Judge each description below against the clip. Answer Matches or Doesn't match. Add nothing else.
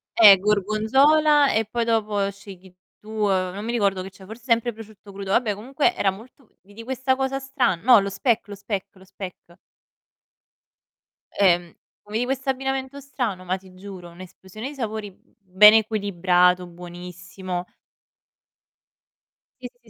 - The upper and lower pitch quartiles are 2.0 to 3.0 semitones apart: Doesn't match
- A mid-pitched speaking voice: Doesn't match